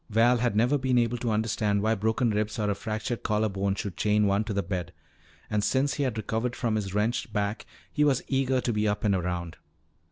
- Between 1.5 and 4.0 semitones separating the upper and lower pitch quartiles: Yes, average, 2.8 semitones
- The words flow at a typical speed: No, fast, 225 wpm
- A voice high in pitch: No, low, 110 Hz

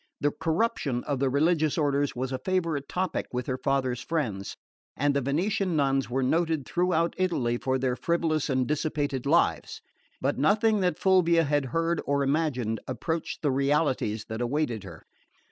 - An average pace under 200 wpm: Yes, average, 160 wpm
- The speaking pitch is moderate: Yes, medium, 145 Hz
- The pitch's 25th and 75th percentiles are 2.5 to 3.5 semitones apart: No, average, 4.1 semitones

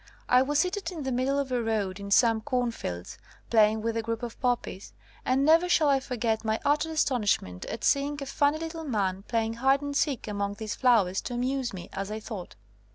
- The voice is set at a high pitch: Yes, high, 245 Hz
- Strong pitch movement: No, average, 4.4 semitones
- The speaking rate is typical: No, fast, 215 wpm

